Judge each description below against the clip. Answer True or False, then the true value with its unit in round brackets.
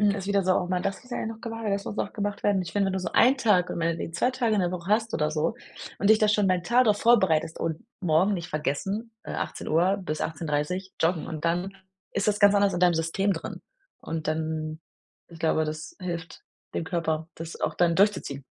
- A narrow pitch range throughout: False (3.9 semitones)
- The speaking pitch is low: False (180 Hz)